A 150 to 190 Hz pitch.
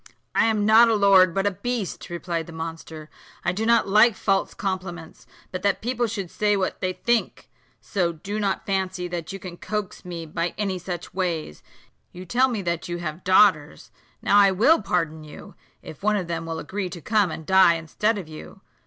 Yes: medium, 185 Hz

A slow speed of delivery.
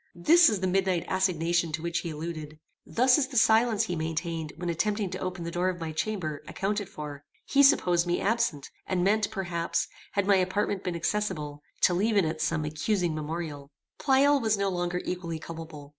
No: average, 190 wpm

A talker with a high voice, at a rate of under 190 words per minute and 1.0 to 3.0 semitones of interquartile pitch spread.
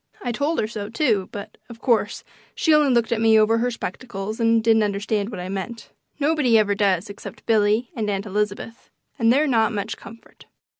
No: high, 225 Hz; average, 195 wpm; narrow, 2.4 semitones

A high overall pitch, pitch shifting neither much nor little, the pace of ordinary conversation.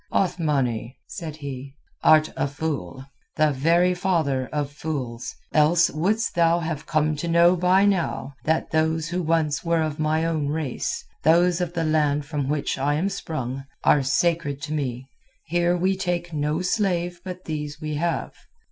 No: medium, 155 Hz; average, 3.1 semitones; average, 165 wpm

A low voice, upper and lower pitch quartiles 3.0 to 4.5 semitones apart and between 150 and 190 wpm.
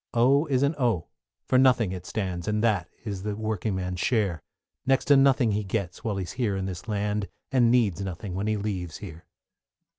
No: low, 105 Hz; average, 4.1 semitones; fast, 205 wpm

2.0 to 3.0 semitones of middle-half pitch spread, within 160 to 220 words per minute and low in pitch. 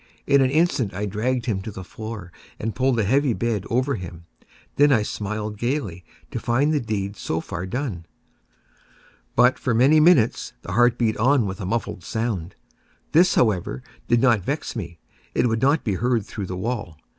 No: average, 4.7 semitones; average, 185 wpm; low, 115 Hz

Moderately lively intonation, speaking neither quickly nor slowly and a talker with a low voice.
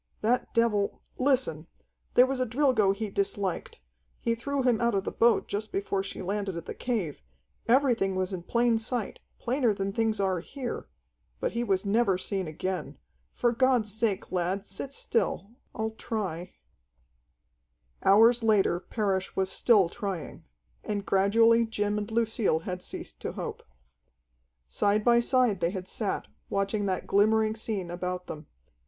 No: average, 3.4 semitones; average, 155 wpm; high, 210 Hz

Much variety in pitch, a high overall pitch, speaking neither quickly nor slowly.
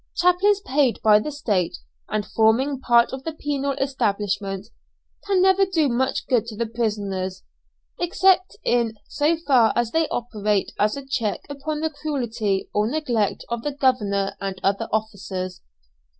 Yes: wide, 5.7 semitones; high, 235 Hz; average, 150 wpm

